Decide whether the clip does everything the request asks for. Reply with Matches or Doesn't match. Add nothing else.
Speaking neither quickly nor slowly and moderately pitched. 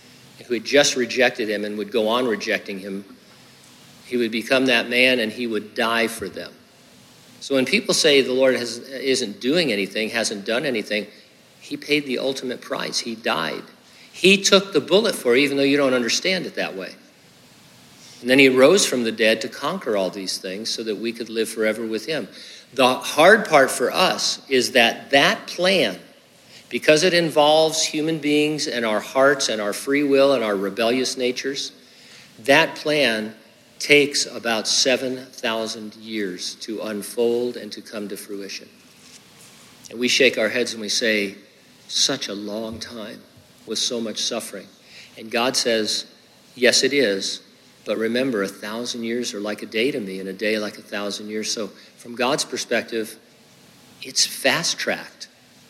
Doesn't match